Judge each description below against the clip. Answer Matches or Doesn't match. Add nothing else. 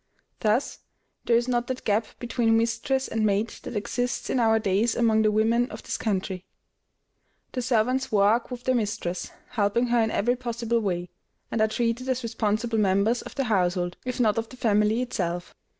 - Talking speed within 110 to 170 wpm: Doesn't match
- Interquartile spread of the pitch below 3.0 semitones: Matches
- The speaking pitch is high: Matches